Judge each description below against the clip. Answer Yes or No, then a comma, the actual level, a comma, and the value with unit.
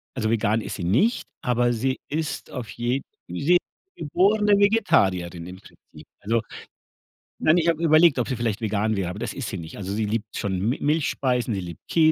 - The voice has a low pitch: Yes, low, 120 Hz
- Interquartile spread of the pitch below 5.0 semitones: No, wide, 7.1 semitones